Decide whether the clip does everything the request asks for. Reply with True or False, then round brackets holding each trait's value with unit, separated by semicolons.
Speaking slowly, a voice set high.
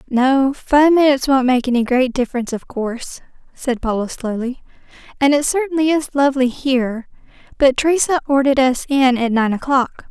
False (160 wpm; 265 Hz)